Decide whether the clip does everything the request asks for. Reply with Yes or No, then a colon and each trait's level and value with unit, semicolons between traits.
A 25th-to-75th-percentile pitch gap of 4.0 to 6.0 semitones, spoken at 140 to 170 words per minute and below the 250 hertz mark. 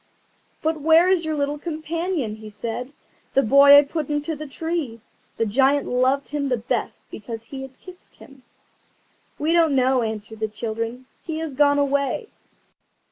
No: average, 4.4 semitones; average, 165 wpm; very high, 280 Hz